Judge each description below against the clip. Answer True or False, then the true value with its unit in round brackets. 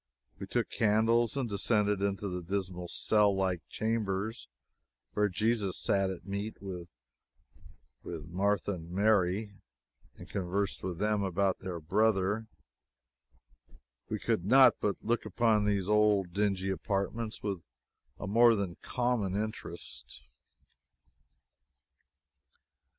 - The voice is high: False (100 Hz)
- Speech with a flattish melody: True (2.3 semitones)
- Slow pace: True (110 wpm)